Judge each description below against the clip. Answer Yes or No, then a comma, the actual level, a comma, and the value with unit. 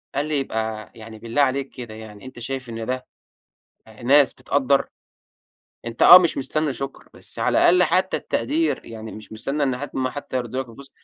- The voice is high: No, low, 130 Hz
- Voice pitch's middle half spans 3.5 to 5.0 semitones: Yes, average, 3.8 semitones